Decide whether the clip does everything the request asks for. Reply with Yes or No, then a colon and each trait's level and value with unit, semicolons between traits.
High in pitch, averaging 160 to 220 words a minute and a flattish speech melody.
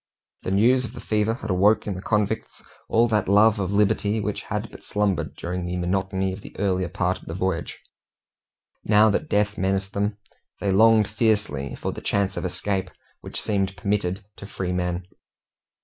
No: low, 100 Hz; average, 180 wpm; narrow, 2.2 semitones